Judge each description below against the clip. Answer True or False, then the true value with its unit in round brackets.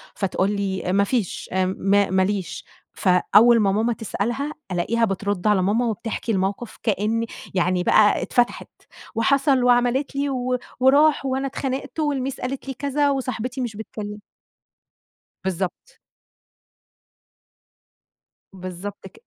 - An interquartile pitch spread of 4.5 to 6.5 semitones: True (5.0 semitones)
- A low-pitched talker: False (225 Hz)